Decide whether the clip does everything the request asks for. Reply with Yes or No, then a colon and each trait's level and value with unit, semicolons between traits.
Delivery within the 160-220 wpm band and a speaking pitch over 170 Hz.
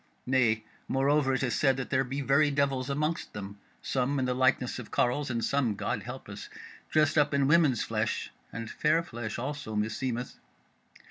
No: average, 180 wpm; low, 130 Hz